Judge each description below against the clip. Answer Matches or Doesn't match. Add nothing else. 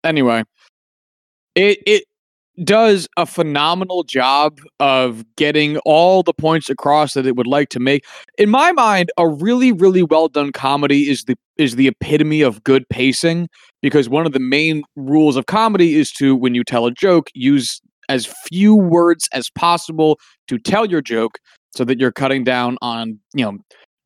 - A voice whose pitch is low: Doesn't match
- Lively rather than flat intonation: Doesn't match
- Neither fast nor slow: Matches